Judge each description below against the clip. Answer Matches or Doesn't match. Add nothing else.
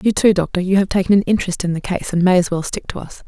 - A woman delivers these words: Matches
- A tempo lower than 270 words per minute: Doesn't match